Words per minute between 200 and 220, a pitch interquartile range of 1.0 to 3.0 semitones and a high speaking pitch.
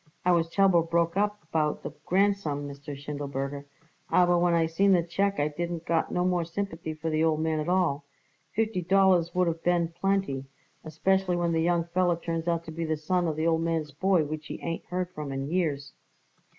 No: fast, 205 wpm; narrow, 2.6 semitones; medium, 170 Hz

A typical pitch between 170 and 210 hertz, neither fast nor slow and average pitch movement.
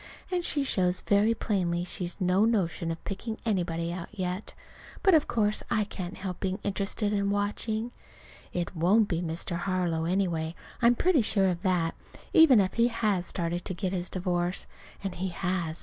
Yes: high, 190 Hz; average, 180 wpm; average, 3.3 semitones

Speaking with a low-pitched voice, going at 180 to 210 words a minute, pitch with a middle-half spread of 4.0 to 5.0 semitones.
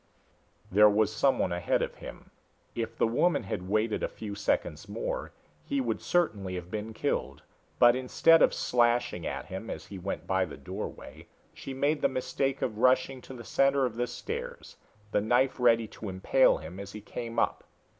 Yes: low, 115 Hz; average, 185 wpm; average, 4.6 semitones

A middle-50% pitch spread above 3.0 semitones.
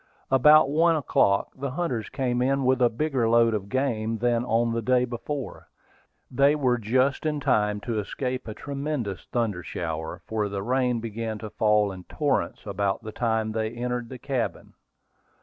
Yes: average, 3.6 semitones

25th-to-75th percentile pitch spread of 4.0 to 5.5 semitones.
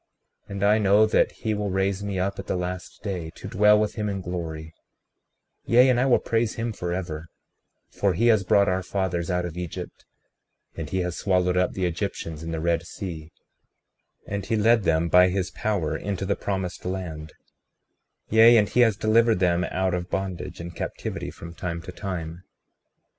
No: average, 3.0 semitones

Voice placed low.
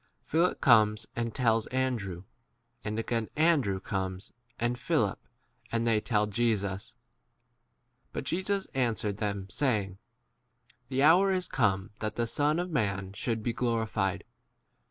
Yes: low, 115 Hz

